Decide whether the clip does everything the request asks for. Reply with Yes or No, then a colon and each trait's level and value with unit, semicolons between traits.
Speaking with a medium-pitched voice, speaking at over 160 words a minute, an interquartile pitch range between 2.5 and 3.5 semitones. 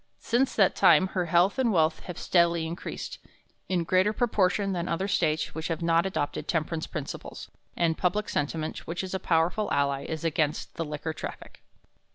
Yes: medium, 170 Hz; average, 175 wpm; average, 2.9 semitones